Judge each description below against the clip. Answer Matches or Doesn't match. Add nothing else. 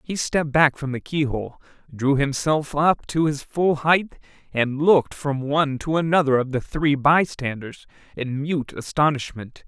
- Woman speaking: Doesn't match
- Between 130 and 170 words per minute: Matches